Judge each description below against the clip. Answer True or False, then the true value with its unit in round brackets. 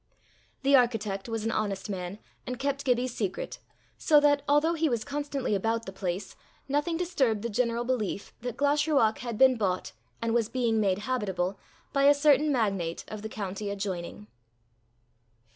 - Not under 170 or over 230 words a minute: False (160 wpm)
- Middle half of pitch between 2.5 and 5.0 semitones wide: False (5.4 semitones)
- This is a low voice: False (230 Hz)